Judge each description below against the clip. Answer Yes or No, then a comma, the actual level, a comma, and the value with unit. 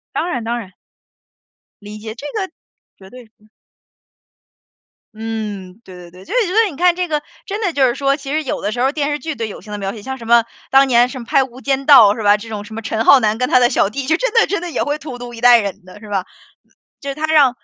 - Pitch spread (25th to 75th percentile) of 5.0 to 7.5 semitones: Yes, wide, 5.4 semitones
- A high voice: Yes, high, 245 Hz